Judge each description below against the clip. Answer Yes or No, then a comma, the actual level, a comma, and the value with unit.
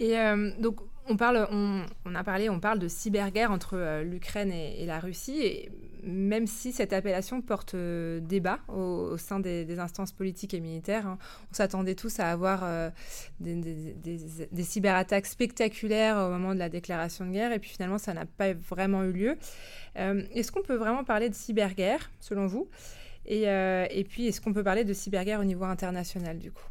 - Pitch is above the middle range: Yes, high, 195 Hz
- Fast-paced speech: No, average, 205 wpm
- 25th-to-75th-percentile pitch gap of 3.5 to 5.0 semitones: No, average, 2.9 semitones